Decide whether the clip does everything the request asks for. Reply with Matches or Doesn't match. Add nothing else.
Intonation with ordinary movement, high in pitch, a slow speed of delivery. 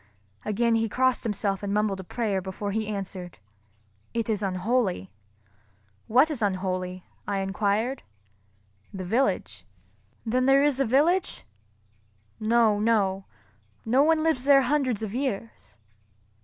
Matches